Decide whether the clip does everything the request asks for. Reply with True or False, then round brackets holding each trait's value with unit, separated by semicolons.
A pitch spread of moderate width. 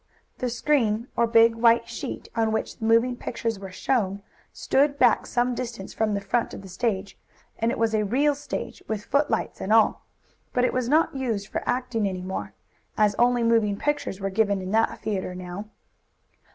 True (3.4 semitones)